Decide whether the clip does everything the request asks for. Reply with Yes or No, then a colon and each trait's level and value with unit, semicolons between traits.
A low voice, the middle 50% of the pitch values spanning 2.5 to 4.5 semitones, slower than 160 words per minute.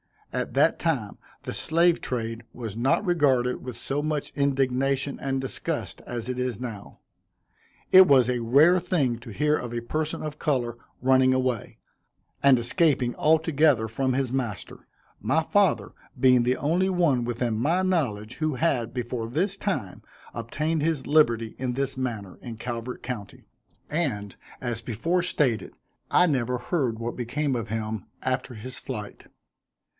Yes: low, 130 Hz; average, 4.2 semitones; average, 150 wpm